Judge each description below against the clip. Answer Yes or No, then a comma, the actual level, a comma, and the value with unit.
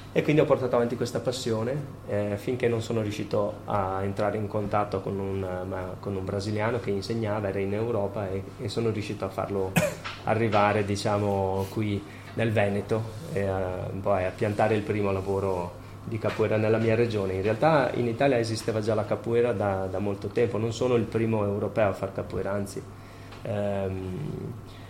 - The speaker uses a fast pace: Yes, fast, 175 wpm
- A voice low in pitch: Yes, low, 105 Hz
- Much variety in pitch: No, average, 2.7 semitones